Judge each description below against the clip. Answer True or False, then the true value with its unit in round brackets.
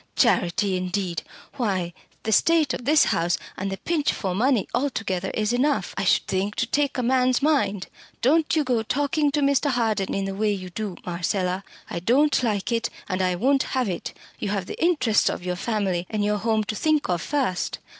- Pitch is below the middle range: False (215 Hz)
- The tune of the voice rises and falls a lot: True (6.0 semitones)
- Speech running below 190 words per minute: False (200 wpm)